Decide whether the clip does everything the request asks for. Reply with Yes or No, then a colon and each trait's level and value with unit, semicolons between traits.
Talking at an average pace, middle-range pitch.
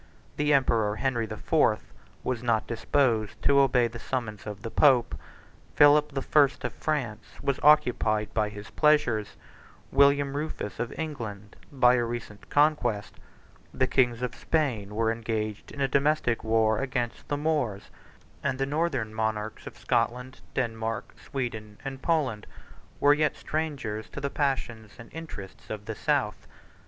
No: average, 150 wpm; low, 120 Hz